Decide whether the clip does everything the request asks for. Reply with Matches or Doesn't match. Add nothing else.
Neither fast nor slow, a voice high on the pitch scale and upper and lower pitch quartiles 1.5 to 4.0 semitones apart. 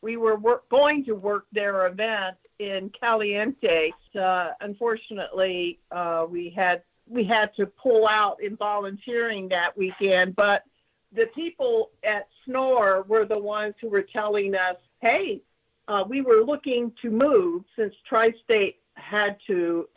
Matches